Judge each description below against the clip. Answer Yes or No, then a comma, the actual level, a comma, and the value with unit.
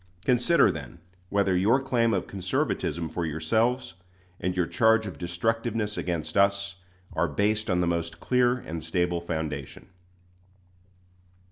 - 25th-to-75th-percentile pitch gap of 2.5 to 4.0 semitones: No, average, 5.0 semitones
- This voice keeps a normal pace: No, slow, 130 wpm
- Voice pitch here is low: Yes, very low, 95 Hz